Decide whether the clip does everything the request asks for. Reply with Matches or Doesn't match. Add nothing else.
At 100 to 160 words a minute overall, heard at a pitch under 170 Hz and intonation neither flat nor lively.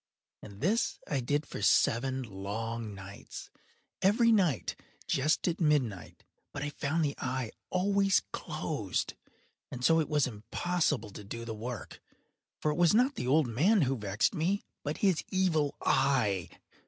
Doesn't match